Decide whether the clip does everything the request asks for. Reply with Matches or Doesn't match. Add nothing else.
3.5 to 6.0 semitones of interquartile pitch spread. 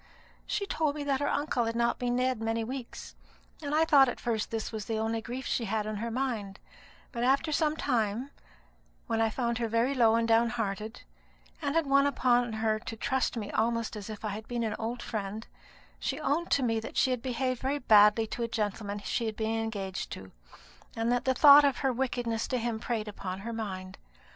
Doesn't match